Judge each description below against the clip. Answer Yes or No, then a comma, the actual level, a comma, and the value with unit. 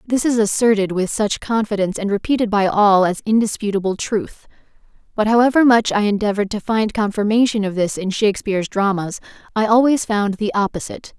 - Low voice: No, high, 210 Hz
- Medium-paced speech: Yes, average, 165 wpm